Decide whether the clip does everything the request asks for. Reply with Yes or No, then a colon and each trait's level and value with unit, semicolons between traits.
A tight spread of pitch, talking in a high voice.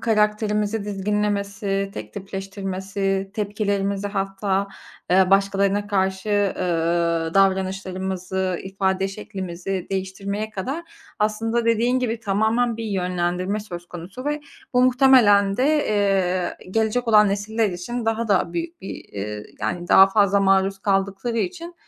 Yes: narrow, 2.2 semitones; high, 200 Hz